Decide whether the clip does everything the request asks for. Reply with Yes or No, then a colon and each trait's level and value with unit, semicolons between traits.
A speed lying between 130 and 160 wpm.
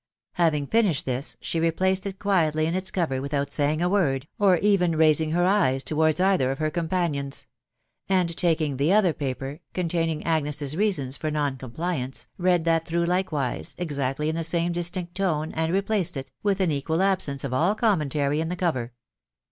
No: average, 185 wpm